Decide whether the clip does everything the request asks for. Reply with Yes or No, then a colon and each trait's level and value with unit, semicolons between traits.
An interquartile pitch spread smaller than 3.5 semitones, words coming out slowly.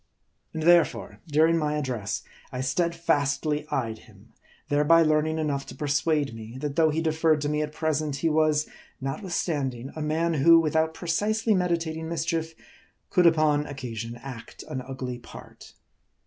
No: average, 2.8 semitones; average, 155 wpm